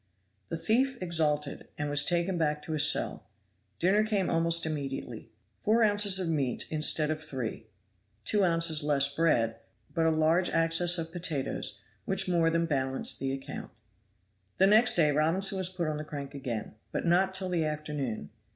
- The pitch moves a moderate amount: Yes, average, 3.5 semitones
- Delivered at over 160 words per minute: Yes, average, 170 wpm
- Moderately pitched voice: Yes, medium, 165 Hz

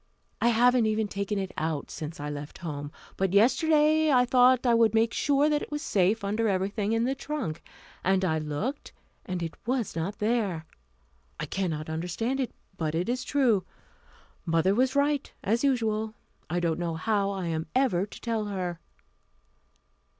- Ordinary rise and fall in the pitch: No, wide, 6.2 semitones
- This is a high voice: Yes, high, 210 Hz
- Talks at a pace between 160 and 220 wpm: Yes, average, 170 wpm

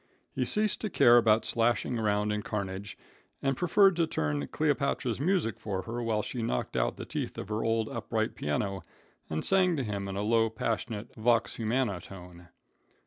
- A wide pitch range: No, average, 3.9 semitones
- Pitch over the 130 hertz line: No, low, 110 Hz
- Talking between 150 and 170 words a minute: No, average, 180 wpm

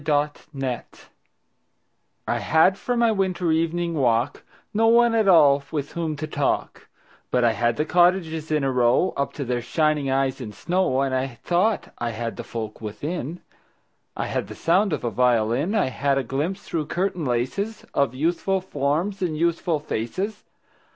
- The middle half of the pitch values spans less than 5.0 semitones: No, wide, 5.5 semitones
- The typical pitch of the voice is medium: Yes, medium, 150 Hz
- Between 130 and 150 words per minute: No, average, 170 wpm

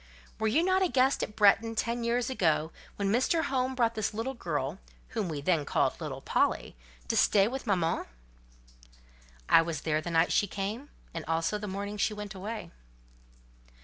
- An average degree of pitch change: No, wide, 5.8 semitones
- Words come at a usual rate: Yes, average, 180 wpm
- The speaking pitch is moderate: No, high, 210 Hz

